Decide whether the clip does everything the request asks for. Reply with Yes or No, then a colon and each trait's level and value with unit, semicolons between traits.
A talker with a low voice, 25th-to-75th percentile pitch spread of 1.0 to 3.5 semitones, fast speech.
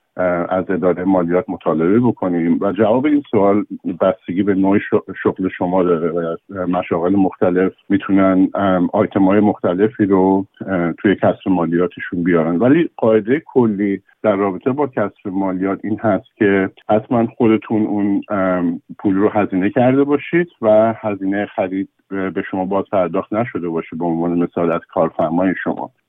No: very low, 95 Hz; narrow, 2.6 semitones; average, 145 wpm